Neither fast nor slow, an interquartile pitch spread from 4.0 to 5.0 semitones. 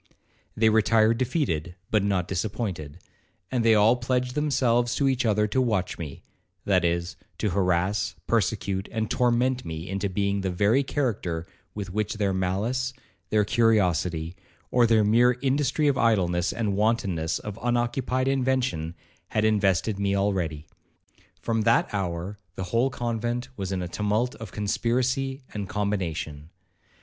Yes: average, 145 wpm; average, 4.4 semitones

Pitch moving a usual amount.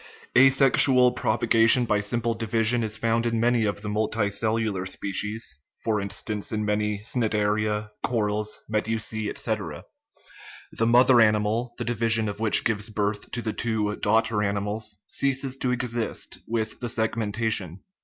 No: narrow, 1.8 semitones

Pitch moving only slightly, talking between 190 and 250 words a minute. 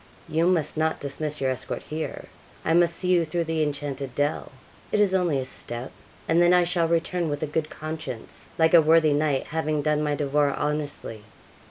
Yes: narrow, 2.3 semitones; average, 195 wpm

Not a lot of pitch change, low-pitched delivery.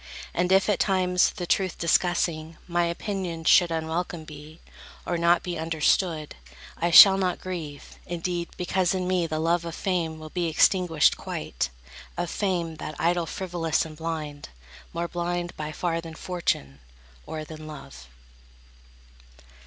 No: narrow, 2.1 semitones; medium, 170 Hz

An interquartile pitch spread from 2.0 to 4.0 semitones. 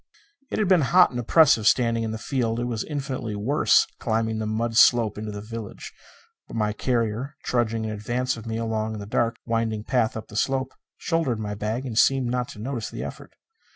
Yes: narrow, 2.6 semitones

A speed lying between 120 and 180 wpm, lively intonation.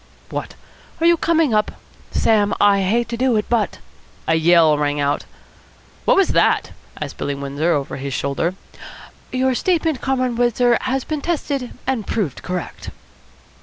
Yes: average, 160 wpm; wide, 8.2 semitones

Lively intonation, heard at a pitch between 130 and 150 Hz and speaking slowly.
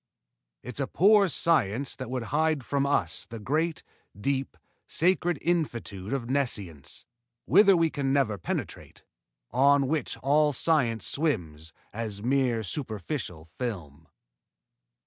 Yes: wide, 5.7 semitones; low, 135 Hz; slow, 120 wpm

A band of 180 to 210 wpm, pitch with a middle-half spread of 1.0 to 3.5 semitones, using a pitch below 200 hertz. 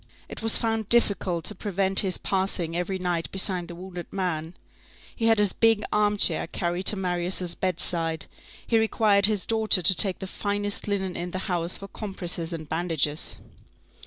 No: average, 165 wpm; average, 2.8 semitones; high, 190 Hz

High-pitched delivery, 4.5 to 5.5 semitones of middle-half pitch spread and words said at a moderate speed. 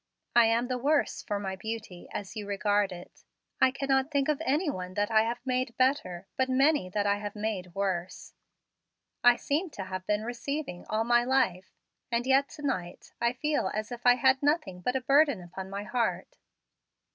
Yes: high, 235 Hz; average, 5.1 semitones; average, 190 wpm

